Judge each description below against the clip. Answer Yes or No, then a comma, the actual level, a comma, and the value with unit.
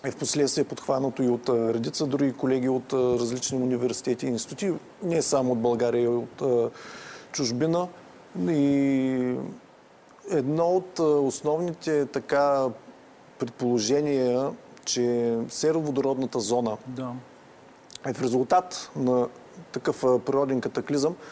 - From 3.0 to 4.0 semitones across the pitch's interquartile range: No, narrow, 2.4 semitones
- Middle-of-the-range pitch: No, low, 130 Hz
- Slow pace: Yes, slow, 105 wpm